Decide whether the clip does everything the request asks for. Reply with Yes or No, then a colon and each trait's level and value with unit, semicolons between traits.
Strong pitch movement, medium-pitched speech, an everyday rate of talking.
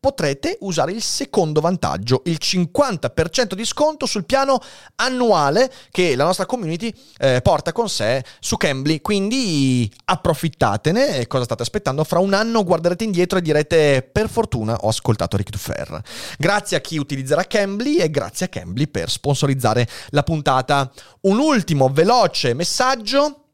Yes: wide, 8.0 semitones; medium, 170 Hz; average, 150 wpm